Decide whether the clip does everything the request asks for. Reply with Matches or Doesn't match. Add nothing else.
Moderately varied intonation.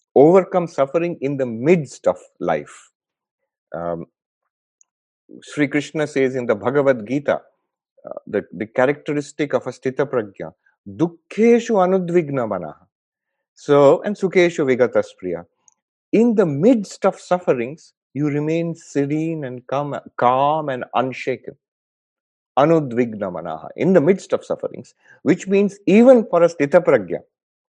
Doesn't match